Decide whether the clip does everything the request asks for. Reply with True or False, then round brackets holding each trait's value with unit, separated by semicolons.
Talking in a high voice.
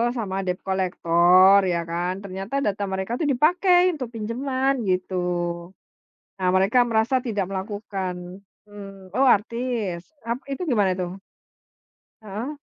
True (205 Hz)